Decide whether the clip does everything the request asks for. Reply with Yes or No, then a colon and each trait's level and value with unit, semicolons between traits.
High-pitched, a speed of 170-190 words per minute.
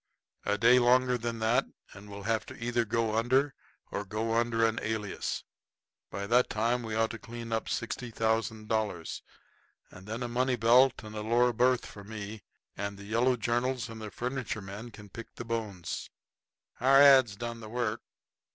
No: low, 115 Hz; average, 175 wpm